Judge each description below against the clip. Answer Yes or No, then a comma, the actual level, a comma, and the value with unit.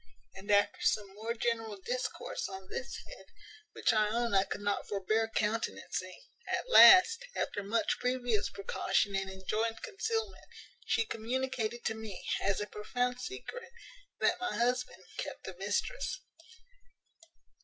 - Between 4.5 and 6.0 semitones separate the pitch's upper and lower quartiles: No, average, 3.7 semitones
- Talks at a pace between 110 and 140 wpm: Yes, slow, 135 wpm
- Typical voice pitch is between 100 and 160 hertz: No, high, 225 Hz